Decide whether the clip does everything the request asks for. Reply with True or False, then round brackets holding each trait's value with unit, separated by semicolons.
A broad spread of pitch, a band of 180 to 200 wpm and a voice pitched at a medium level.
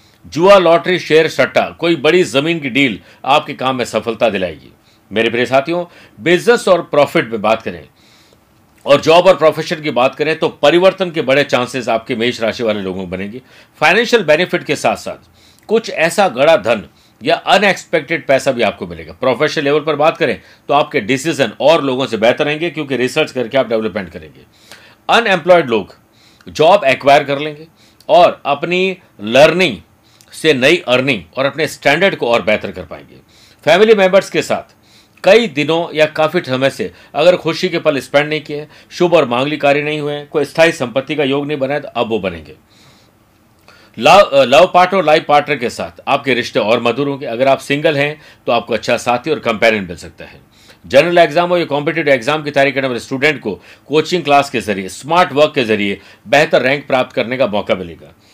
True (5.9 semitones; 185 wpm; 145 Hz)